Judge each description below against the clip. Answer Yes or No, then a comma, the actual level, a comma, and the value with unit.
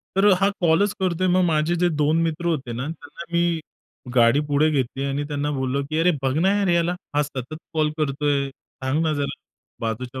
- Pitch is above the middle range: No, medium, 150 Hz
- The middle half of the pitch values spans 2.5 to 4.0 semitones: Yes, average, 3.7 semitones